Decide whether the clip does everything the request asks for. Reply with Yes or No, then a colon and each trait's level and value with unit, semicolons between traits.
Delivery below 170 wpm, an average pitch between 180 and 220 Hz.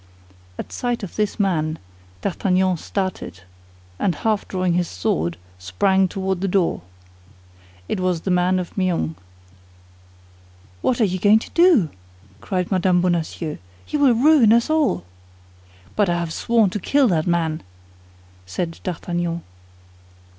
Yes: slow, 135 wpm; medium, 185 Hz